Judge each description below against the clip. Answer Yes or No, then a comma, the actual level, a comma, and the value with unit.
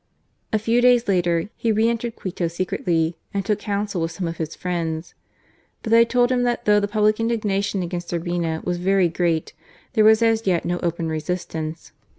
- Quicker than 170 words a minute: Yes, average, 185 wpm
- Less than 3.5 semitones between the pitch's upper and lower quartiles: No, average, 4.4 semitones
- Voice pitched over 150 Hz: Yes, high, 190 Hz